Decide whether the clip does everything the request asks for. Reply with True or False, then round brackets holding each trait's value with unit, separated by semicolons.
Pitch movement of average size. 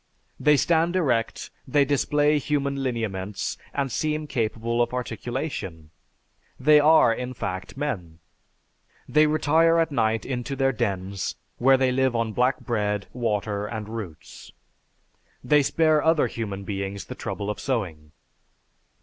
False (5.8 semitones)